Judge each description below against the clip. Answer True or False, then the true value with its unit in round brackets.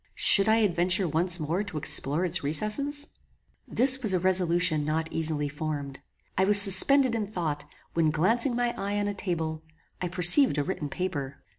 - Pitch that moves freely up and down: False (4.8 semitones)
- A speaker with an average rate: True (170 wpm)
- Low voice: False (180 Hz)